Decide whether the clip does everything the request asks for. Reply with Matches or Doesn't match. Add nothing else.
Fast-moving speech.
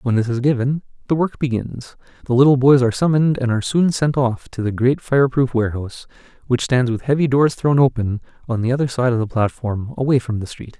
Matches